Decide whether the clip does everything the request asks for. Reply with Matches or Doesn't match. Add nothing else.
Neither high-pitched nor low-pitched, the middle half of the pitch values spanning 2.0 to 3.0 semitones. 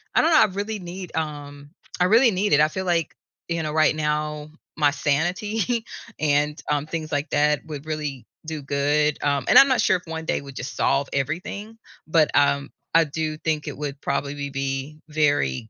Matches